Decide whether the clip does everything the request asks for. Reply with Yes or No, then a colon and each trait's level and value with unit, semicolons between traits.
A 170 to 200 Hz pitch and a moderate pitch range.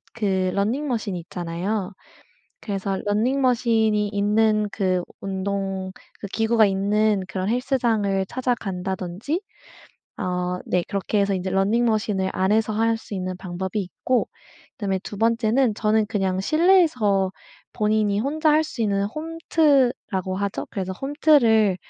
No: high, 210 Hz; average, 3.3 semitones